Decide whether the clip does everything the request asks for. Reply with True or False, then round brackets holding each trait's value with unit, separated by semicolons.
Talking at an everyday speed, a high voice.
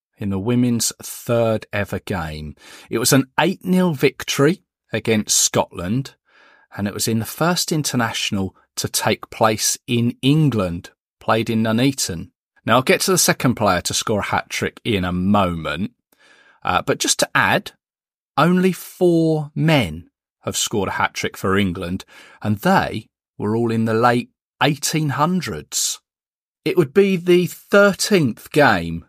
False (145 wpm; 120 Hz)